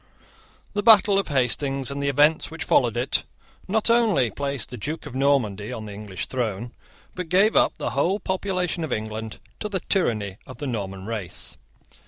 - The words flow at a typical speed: Yes, average, 180 wpm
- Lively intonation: Yes, wide, 8.8 semitones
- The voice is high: No, medium, 140 Hz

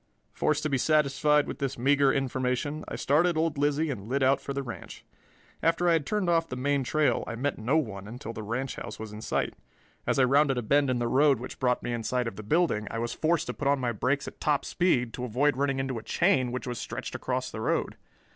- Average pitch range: Yes, average, 3.4 semitones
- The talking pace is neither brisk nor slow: No, fast, 250 wpm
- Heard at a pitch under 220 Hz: Yes, low, 135 Hz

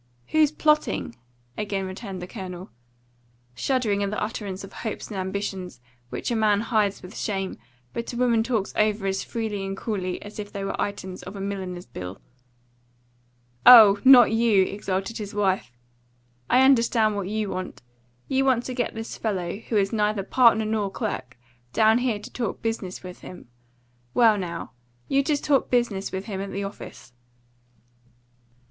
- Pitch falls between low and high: No, high, 205 Hz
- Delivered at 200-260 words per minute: No, average, 165 wpm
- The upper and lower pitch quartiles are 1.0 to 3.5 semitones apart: Yes, average, 3.1 semitones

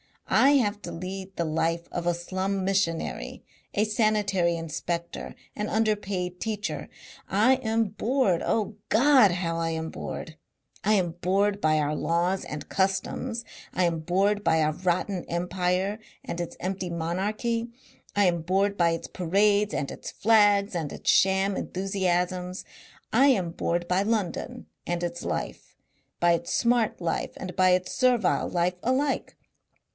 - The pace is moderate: Yes, average, 150 wpm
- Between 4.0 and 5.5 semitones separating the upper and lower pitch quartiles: No, average, 3.2 semitones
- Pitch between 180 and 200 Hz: Yes, high, 190 Hz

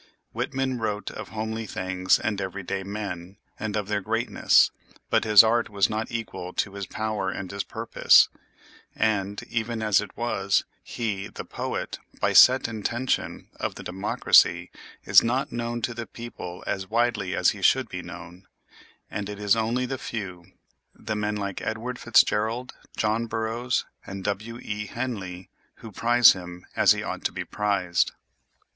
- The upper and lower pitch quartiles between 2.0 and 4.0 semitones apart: Yes, average, 3.0 semitones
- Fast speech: No, average, 160 wpm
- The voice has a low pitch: Yes, low, 105 Hz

